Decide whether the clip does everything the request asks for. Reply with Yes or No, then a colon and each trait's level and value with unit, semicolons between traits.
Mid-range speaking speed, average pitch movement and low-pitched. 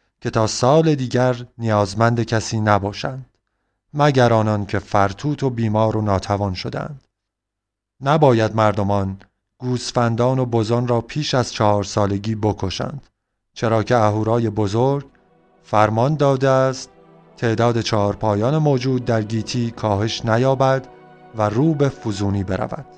Yes: average, 120 wpm; average, 3.4 semitones; low, 115 Hz